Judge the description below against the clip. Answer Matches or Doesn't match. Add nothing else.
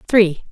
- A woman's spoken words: Matches